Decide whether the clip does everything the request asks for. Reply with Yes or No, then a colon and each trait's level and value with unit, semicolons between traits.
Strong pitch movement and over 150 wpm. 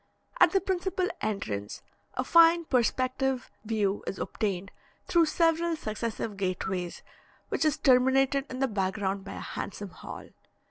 No: wide, 8.0 semitones; slow, 135 wpm